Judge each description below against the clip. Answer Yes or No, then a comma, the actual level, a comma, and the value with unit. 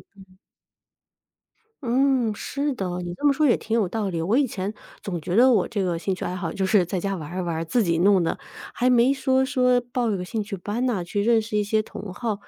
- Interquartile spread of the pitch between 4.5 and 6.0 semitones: Yes, average, 5.2 semitones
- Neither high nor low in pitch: No, high, 210 Hz